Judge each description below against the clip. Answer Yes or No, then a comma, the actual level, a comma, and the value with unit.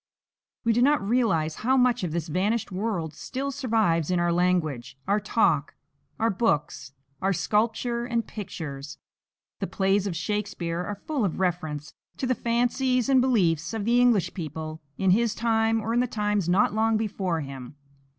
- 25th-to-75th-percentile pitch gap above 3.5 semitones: Yes, wide, 5.6 semitones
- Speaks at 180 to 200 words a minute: No, average, 170 wpm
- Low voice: No, high, 205 Hz